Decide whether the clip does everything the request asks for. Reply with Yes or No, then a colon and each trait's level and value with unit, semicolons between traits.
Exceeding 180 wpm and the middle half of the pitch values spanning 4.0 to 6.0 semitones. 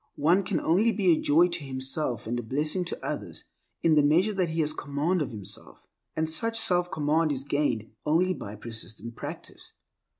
Yes: average, 190 wpm; average, 5.0 semitones